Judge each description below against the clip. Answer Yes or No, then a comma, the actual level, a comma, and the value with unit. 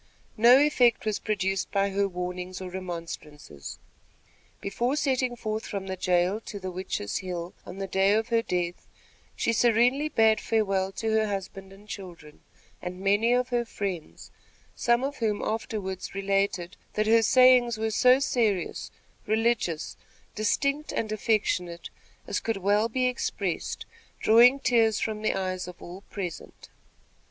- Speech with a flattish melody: No, average, 3.7 semitones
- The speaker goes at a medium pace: Yes, average, 150 wpm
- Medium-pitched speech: No, high, 210 Hz